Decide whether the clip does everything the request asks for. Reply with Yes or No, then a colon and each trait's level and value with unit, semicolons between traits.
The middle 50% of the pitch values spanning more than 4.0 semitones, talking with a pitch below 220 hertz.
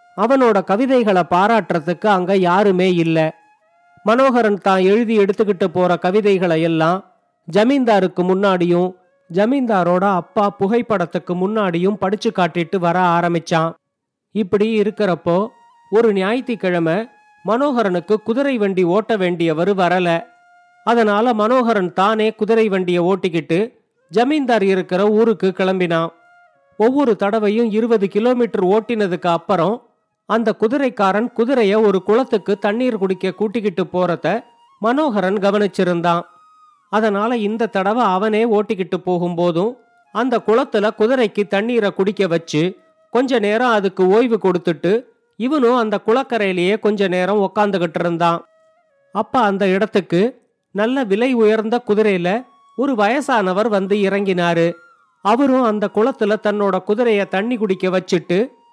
No: average, 3.7 semitones; high, 205 Hz